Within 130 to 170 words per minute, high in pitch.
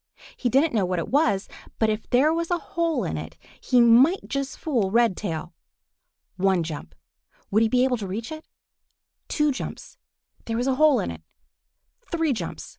No: average, 180 wpm; high, 240 Hz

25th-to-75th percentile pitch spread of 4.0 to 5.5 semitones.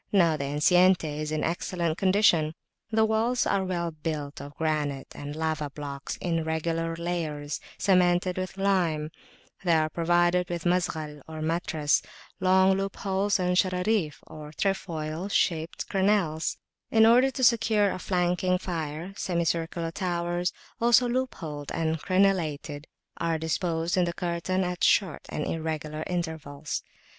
No: average, 3.0 semitones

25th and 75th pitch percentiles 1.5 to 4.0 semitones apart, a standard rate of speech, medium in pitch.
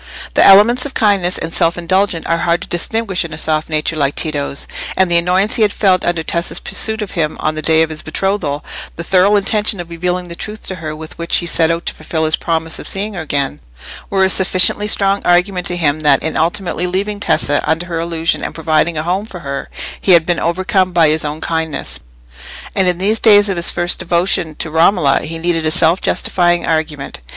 No: average, 3.1 semitones; fast, 220 wpm; medium, 170 Hz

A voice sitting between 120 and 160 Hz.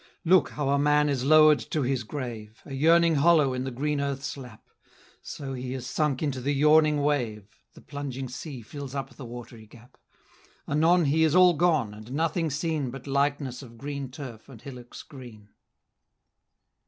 Yes: medium, 140 Hz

